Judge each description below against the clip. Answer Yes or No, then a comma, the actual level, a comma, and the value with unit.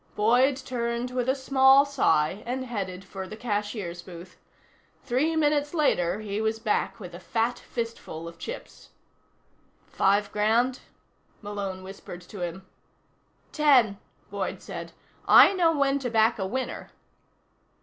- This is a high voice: Yes, high, 225 Hz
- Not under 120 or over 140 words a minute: Yes, slow, 135 wpm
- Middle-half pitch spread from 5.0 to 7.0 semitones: Yes, average, 5.3 semitones